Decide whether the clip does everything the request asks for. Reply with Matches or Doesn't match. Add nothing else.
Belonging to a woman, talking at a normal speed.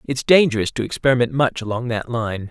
Doesn't match